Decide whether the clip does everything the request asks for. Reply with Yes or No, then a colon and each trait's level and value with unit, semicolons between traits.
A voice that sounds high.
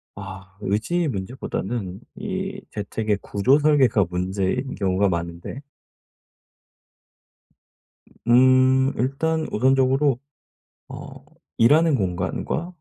No: low, 125 Hz